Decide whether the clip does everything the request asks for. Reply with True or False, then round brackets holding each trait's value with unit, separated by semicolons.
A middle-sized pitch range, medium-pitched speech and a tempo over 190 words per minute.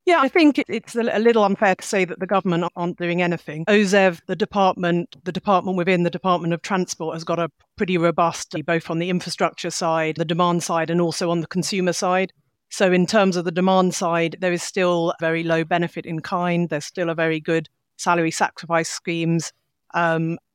False (2.1 semitones; 175 Hz; 200 wpm)